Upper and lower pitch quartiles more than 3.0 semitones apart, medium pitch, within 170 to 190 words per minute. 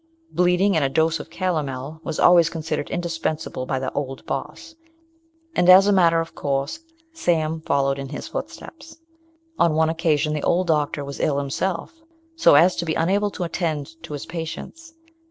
Yes: average, 3.4 semitones; medium, 160 Hz; average, 175 wpm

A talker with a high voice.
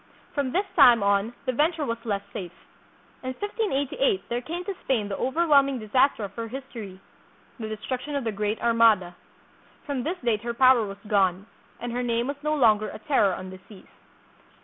Yes: high, 240 Hz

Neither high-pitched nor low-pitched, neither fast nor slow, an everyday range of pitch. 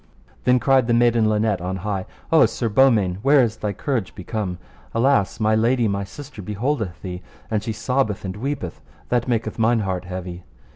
No: low, 110 Hz; average, 180 wpm; average, 4.1 semitones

